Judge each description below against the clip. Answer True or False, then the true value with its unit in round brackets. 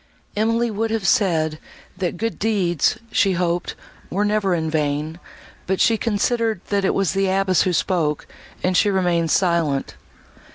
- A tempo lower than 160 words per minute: True (150 wpm)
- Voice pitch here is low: False (190 Hz)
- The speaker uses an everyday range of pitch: True (3.5 semitones)